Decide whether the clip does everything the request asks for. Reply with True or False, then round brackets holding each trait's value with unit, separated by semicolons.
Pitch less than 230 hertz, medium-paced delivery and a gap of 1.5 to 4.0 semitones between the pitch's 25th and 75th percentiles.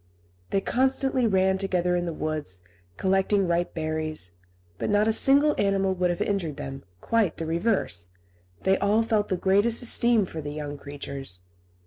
False (190 Hz; 160 wpm; 5.0 semitones)